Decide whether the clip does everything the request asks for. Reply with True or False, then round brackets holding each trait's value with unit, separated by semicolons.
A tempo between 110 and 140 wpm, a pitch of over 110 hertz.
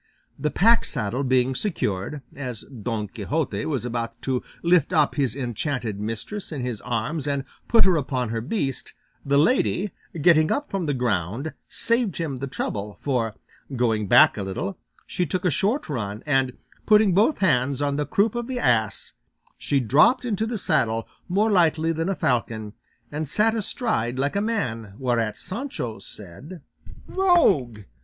False (165 wpm; 140 Hz)